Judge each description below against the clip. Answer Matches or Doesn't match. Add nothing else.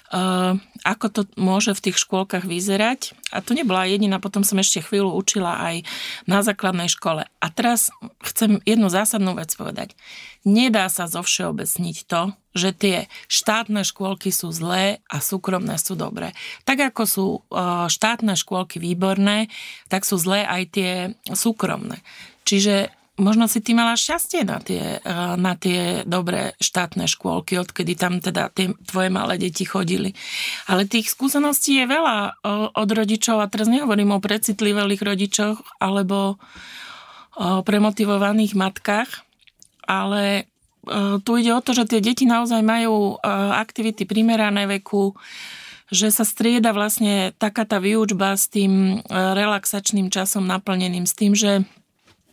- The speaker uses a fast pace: Doesn't match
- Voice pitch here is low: Doesn't match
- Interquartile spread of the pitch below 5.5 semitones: Matches